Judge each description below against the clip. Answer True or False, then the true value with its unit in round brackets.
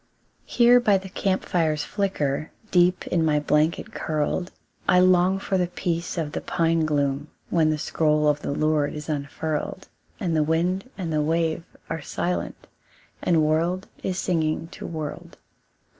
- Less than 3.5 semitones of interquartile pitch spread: True (2.9 semitones)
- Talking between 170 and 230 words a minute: False (160 wpm)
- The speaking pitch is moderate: True (165 Hz)